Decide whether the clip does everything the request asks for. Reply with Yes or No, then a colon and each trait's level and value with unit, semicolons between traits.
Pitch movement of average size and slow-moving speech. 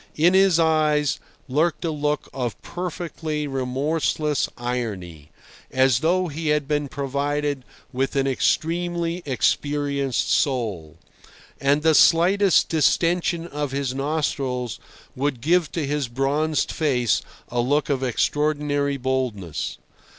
Yes: average, 3.3 semitones; slow, 115 wpm